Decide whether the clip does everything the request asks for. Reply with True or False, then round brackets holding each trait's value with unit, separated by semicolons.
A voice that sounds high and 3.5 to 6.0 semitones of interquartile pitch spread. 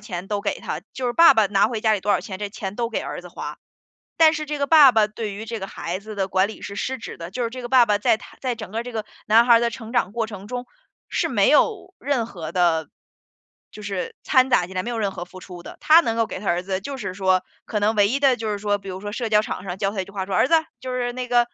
True (215 Hz; 3.8 semitones)